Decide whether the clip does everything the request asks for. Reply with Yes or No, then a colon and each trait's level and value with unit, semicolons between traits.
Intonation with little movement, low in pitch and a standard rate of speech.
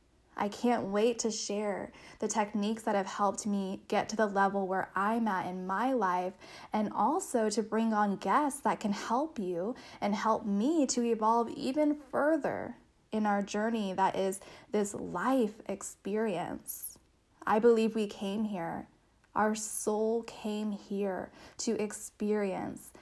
No: narrow, 2.3 semitones; high, 215 Hz; average, 150 wpm